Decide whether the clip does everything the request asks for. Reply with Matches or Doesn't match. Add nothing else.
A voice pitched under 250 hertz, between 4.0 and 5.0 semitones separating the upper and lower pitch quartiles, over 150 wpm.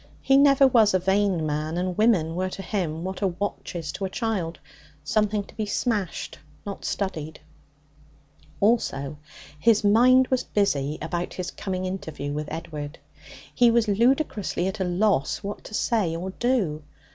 Matches